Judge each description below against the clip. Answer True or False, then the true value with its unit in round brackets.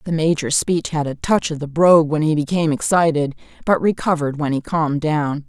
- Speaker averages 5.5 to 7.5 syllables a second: True (5.8 syllables/s)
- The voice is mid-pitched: True (155 Hz)